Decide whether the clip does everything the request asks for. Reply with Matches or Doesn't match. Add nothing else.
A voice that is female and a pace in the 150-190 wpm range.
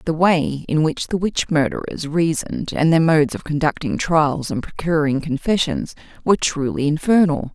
Matches